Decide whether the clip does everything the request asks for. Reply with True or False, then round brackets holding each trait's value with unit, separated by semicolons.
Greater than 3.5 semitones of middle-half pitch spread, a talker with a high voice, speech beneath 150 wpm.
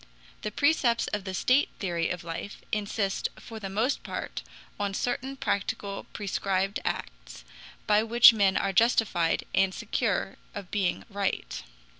False (2.9 semitones; 200 Hz; 140 wpm)